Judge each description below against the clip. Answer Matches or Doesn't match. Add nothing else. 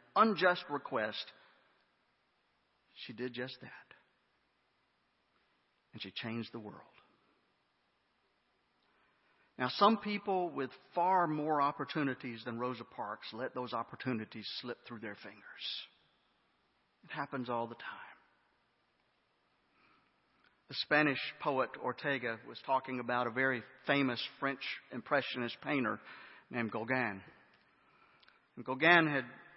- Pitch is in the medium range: Doesn't match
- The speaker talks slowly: Matches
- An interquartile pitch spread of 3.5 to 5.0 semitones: Matches